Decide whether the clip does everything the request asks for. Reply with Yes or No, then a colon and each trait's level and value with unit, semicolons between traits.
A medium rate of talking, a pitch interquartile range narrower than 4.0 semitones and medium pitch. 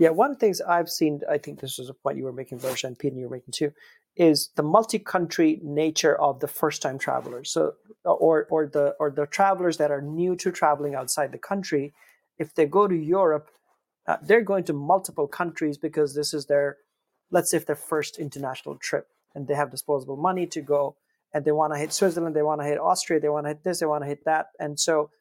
No: fast, 225 wpm; average, 2.8 semitones; medium, 155 Hz